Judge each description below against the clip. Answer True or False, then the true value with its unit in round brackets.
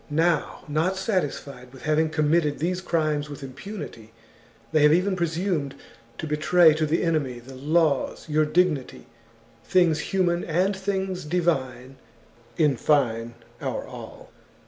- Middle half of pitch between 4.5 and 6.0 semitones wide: False (3.6 semitones)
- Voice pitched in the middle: True (155 Hz)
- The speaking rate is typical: False (130 wpm)